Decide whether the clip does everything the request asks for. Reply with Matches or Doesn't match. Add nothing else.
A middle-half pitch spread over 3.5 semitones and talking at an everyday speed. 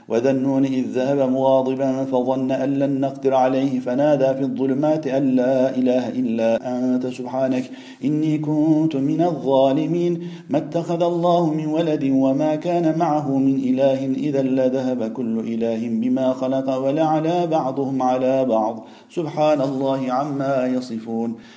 Doesn't match